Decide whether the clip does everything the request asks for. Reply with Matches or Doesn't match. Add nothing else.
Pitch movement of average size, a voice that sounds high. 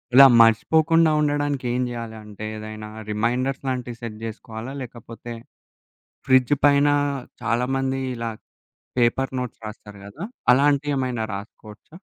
Doesn't match